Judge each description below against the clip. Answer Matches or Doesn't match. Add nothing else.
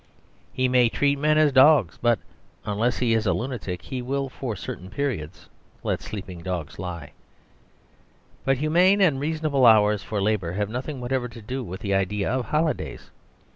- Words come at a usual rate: Matches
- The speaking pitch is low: Matches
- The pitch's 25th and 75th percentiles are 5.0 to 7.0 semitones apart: Matches